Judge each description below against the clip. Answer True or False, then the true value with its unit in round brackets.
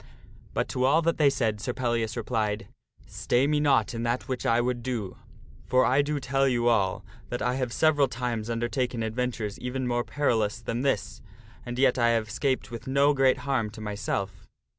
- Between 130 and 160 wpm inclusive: False (195 wpm)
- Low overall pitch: True (125 Hz)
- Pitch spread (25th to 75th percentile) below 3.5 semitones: True (2.6 semitones)